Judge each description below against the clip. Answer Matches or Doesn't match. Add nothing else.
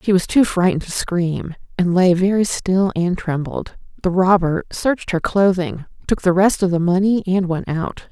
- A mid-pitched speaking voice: Matches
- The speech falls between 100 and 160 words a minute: Doesn't match